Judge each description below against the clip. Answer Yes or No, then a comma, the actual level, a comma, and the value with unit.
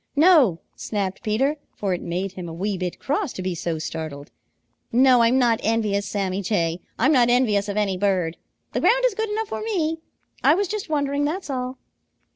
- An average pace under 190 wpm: No, average, 195 wpm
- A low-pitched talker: No, high, 225 Hz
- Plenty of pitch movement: Yes, wide, 7.6 semitones